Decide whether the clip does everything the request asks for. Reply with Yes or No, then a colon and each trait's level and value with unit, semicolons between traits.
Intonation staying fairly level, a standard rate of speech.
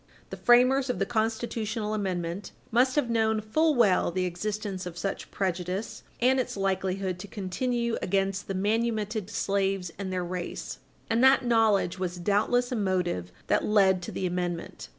No: average, 3.7 semitones; average, 160 wpm